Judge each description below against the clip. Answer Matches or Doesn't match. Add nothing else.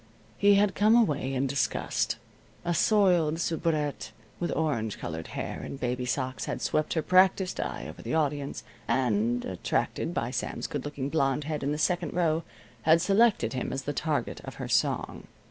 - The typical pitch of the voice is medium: Matches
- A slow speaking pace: Doesn't match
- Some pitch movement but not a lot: Matches